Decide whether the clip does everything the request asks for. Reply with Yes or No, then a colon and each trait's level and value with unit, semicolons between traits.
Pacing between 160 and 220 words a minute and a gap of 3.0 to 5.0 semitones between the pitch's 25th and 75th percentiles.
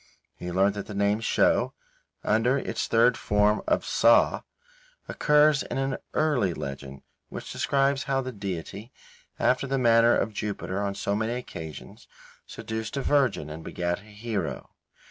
No: average, 150 wpm; average, 4.7 semitones